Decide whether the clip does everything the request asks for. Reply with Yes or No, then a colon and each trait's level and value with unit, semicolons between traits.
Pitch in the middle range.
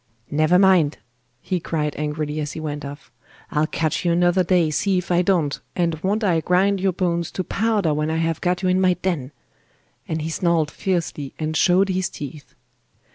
Yes: medium, 170 Hz